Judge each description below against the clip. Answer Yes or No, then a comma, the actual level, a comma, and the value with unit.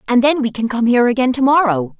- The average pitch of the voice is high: Yes, high, 245 Hz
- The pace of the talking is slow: No, fast, 270 wpm